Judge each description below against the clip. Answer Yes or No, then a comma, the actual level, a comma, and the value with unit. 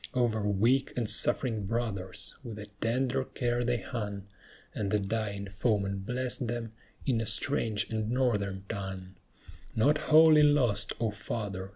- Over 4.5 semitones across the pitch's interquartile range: No, average, 3.4 semitones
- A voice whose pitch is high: No, low, 110 Hz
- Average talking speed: Yes, average, 145 wpm